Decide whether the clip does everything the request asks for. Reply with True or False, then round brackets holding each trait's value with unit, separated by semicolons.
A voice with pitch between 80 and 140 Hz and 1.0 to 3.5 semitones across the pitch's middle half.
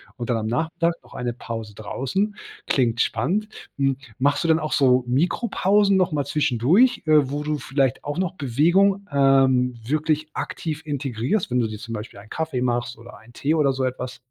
False (135 Hz; 4.6 semitones)